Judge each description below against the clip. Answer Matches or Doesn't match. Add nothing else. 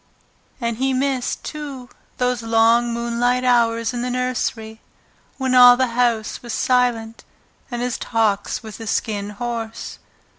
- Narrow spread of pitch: Matches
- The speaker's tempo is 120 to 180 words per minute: Matches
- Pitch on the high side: Matches